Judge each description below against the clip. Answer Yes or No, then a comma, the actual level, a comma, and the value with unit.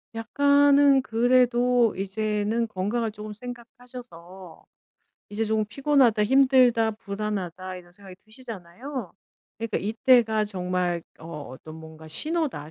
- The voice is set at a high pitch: Yes, high, 215 Hz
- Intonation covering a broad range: No, average, 4.9 semitones